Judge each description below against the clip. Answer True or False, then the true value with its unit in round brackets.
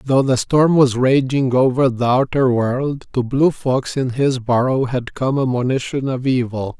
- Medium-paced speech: True (185 wpm)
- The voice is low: True (130 Hz)